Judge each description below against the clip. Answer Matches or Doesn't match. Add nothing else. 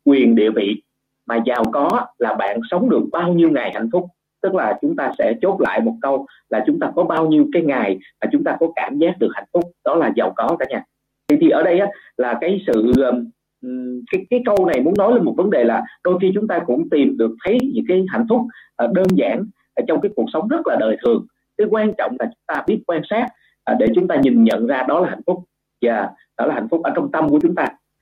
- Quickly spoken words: Matches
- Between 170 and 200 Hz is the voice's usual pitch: Matches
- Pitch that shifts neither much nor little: Doesn't match